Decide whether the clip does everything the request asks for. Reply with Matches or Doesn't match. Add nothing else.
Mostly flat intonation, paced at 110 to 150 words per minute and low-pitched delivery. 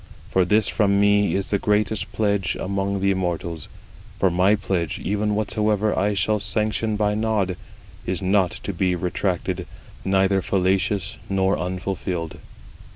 Matches